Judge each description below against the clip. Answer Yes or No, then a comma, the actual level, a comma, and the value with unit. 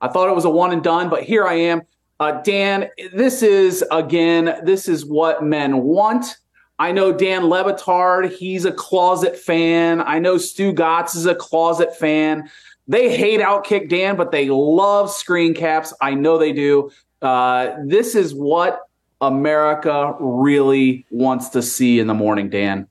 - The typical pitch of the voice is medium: Yes, medium, 165 Hz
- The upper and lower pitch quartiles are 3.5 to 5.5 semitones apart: Yes, average, 4.5 semitones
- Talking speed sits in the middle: Yes, average, 170 wpm